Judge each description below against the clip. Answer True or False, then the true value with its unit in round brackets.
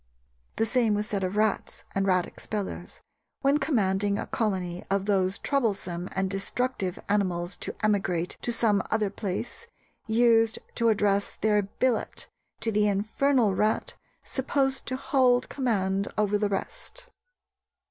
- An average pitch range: True (3.4 semitones)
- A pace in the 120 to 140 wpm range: True (135 wpm)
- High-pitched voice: True (210 Hz)